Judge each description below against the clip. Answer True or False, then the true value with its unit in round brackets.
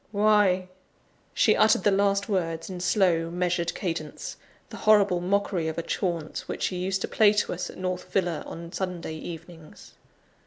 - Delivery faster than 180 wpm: False (165 wpm)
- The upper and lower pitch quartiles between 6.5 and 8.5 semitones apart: False (2.9 semitones)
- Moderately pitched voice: True (180 Hz)